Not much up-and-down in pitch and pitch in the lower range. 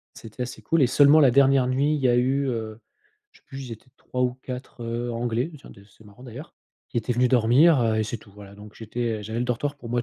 No: average, 3.0 semitones; low, 125 Hz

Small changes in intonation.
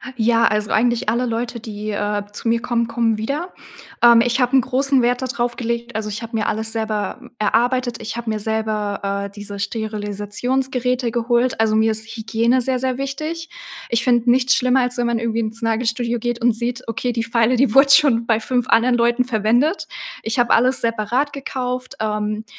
Yes: narrow, 2.2 semitones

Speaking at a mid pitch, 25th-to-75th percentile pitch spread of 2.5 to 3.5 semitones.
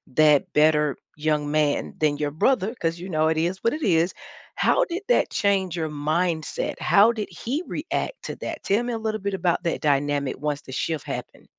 No: medium, 165 Hz; average, 5.0 semitones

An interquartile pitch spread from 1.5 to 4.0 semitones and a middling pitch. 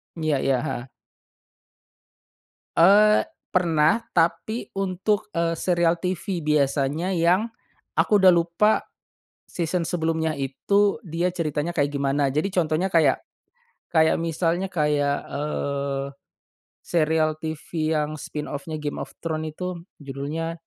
Yes: average, 3.0 semitones; medium, 165 Hz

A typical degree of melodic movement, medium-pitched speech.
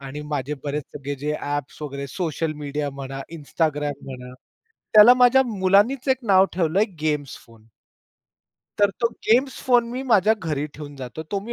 No: wide, 6.5 semitones; medium, 155 Hz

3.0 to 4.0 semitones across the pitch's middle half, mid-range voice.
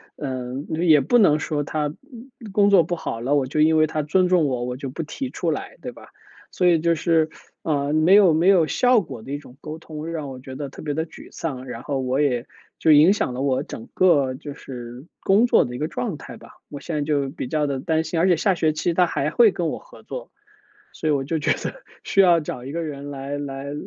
Yes: average, 3.7 semitones; medium, 155 Hz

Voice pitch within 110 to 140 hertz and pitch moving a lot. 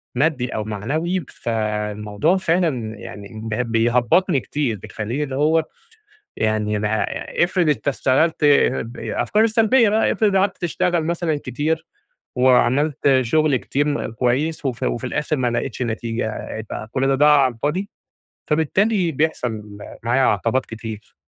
Yes: low, 135 Hz; wide, 6.1 semitones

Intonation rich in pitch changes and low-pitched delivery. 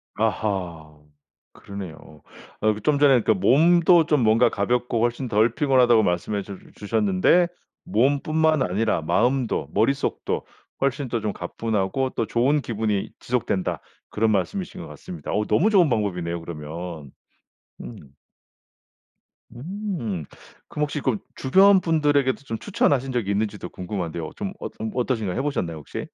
Yes: wide, 6.0 semitones; low, 115 Hz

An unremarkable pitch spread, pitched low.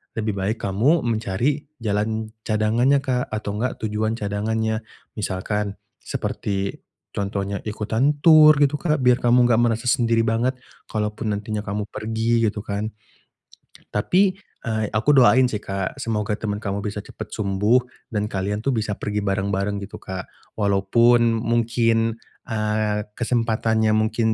No: narrow, 2.3 semitones; low, 110 Hz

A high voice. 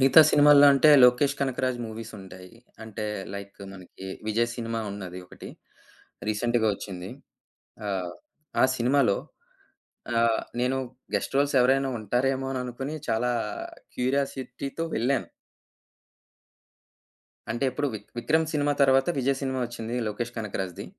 No: low, 125 Hz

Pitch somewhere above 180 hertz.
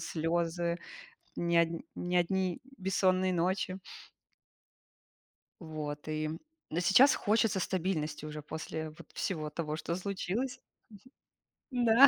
No: medium, 175 Hz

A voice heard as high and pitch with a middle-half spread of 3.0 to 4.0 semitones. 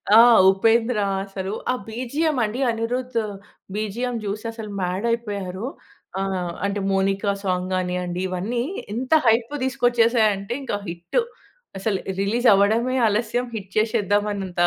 Yes: high, 215 Hz; average, 3.4 semitones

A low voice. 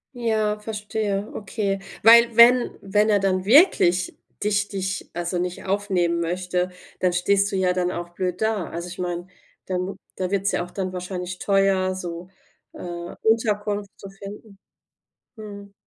No: high, 195 Hz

